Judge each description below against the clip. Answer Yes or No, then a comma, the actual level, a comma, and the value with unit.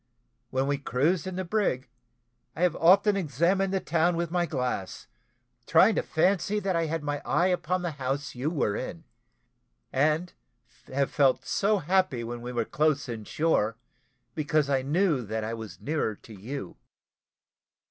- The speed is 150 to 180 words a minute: Yes, average, 165 wpm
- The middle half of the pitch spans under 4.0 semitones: No, wide, 5.5 semitones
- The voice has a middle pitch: Yes, medium, 155 Hz